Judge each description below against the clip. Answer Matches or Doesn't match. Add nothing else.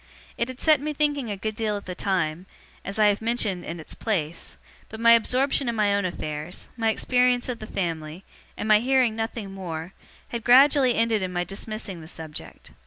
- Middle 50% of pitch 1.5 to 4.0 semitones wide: Doesn't match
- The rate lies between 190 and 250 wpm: Matches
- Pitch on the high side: Matches